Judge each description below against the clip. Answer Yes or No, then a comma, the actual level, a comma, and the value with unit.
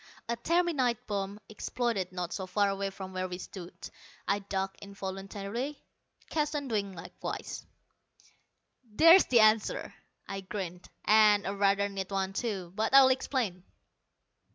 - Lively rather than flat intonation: No, average, 3.4 semitones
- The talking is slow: Yes, slow, 130 wpm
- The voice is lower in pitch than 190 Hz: No, high, 200 Hz